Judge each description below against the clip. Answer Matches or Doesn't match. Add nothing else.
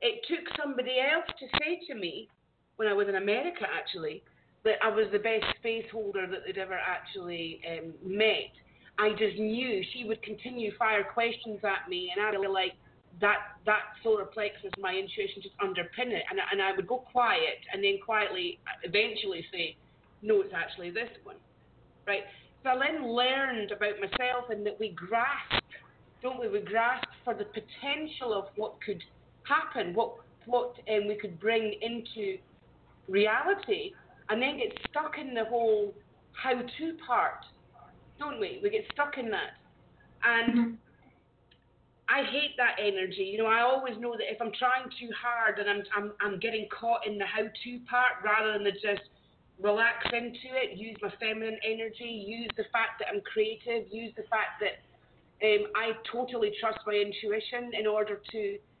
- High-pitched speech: Matches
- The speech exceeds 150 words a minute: Matches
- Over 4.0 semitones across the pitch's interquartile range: Doesn't match